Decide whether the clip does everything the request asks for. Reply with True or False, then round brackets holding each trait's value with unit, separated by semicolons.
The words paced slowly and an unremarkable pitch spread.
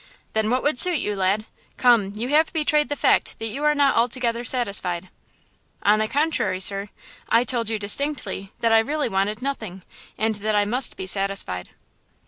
False (180 wpm; 4.9 semitones)